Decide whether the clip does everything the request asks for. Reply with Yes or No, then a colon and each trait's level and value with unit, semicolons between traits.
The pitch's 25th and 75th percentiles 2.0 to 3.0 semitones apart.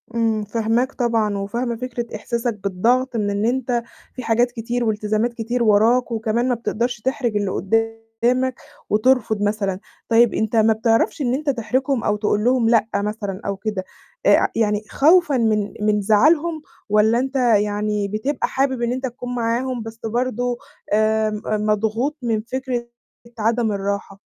Yes: narrow, 2.6 semitones